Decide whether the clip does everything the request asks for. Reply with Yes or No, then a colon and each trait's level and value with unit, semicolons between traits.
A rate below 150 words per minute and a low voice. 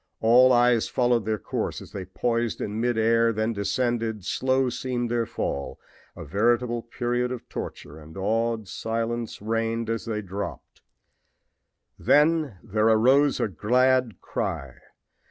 Yes: slow, 135 wpm; low, 115 Hz